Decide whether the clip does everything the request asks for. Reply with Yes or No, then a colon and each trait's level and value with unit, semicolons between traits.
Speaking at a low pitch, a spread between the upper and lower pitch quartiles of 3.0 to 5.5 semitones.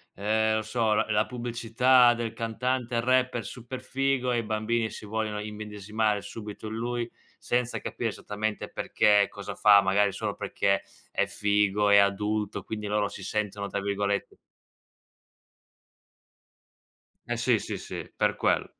No: low, 110 Hz; narrow, 2.4 semitones